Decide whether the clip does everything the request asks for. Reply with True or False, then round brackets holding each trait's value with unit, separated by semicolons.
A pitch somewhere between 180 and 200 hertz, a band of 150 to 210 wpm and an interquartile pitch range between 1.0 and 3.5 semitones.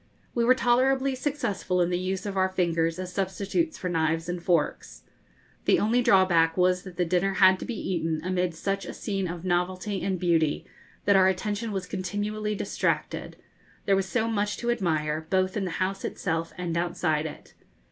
True (185 Hz; 185 wpm; 2.8 semitones)